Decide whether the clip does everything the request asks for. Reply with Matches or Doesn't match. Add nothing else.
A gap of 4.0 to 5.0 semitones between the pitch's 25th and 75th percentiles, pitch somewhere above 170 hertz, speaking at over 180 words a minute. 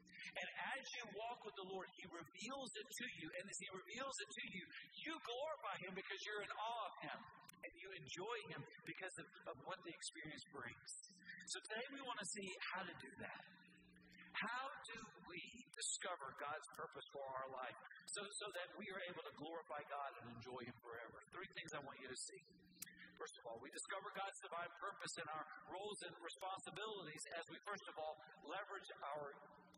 Matches